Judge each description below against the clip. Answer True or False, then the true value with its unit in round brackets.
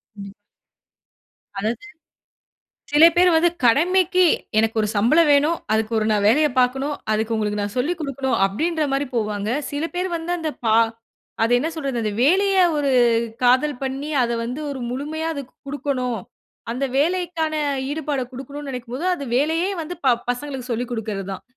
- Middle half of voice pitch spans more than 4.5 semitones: True (5.1 semitones)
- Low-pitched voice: False (275 Hz)